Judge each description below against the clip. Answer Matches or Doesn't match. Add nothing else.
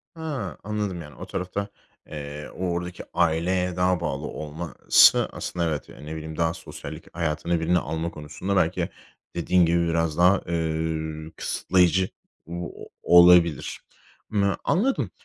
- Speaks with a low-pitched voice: Matches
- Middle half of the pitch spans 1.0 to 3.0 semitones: Matches